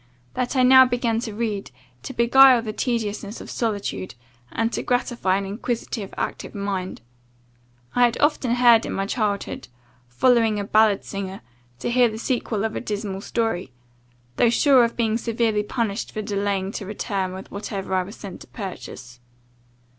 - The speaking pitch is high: Yes, high, 215 Hz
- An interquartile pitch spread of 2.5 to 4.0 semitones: Yes, average, 3.2 semitones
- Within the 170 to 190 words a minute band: No, average, 160 wpm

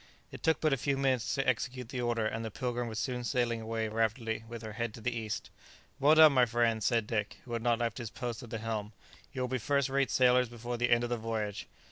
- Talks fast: Yes, fast, 255 wpm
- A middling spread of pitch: No, narrow, 2.1 semitones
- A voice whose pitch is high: No, low, 120 Hz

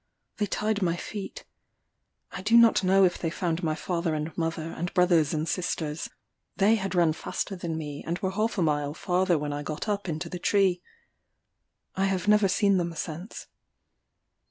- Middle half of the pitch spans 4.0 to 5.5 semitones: No, average, 3.2 semitones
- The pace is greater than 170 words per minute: Yes, average, 180 wpm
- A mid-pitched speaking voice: Yes, medium, 175 Hz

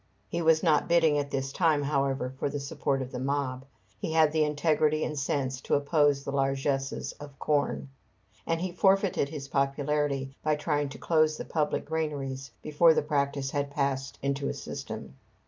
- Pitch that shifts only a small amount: Yes, narrow, 2.0 semitones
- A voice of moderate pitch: Yes, medium, 145 Hz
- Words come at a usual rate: Yes, average, 180 wpm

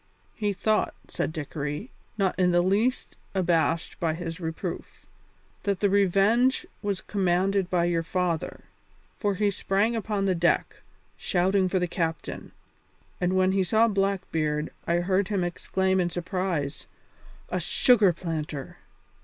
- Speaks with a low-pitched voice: No, medium, 185 Hz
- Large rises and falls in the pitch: No, average, 2.7 semitones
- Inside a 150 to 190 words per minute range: No, slow, 135 wpm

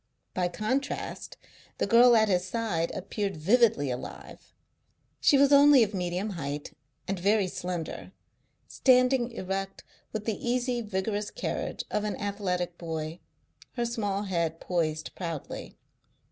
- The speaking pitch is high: Yes, high, 200 Hz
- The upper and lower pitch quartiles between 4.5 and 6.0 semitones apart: Yes, average, 4.8 semitones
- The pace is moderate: No, slow, 130 wpm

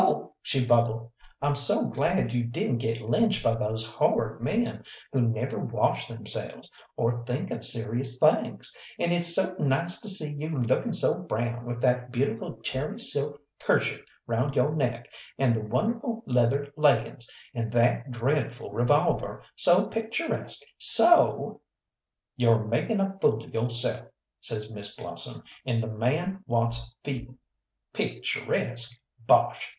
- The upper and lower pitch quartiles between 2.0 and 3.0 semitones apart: No, average, 4.2 semitones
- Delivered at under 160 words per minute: Yes, average, 145 wpm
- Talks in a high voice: No, low, 125 Hz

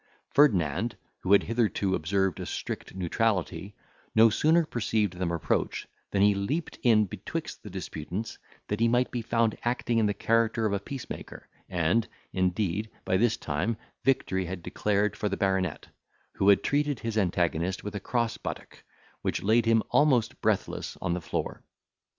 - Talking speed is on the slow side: No, average, 160 wpm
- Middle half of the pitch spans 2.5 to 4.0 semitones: Yes, average, 3.6 semitones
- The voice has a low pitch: Yes, low, 105 Hz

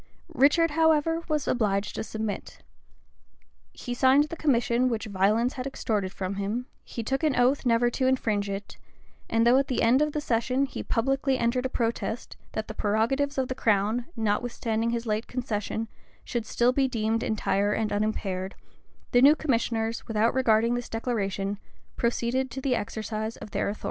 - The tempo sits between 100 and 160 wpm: No, average, 170 wpm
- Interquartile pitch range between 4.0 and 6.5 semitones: No, average, 3.2 semitones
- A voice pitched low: No, high, 235 Hz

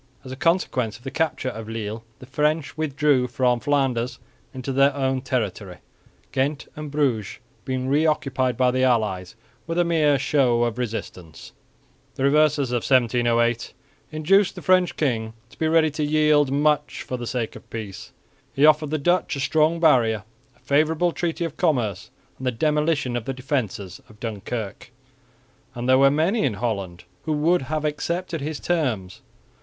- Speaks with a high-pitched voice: No, low, 135 Hz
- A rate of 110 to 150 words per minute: No, average, 170 wpm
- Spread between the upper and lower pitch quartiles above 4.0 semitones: Yes, average, 4.4 semitones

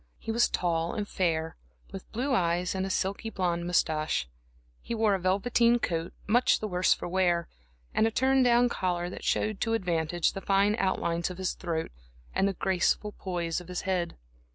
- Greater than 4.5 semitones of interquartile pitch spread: No, average, 3.8 semitones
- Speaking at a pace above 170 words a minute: Yes, average, 190 wpm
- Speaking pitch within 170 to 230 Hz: Yes, medium, 185 Hz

